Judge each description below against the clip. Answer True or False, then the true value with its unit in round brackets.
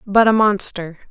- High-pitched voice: True (200 Hz)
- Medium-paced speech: True (165 wpm)